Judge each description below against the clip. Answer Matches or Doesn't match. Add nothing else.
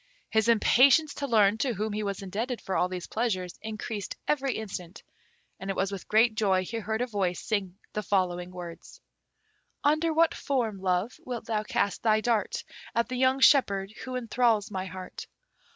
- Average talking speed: Matches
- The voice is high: Matches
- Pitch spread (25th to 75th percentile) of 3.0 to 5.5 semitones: Matches